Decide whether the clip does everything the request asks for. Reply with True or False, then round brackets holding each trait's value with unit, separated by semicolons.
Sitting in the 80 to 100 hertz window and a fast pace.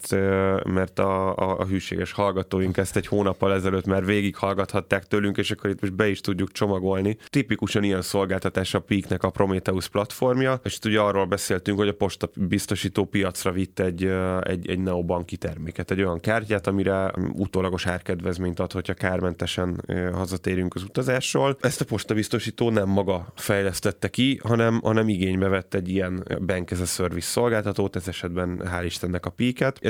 True (95 Hz; 160 wpm)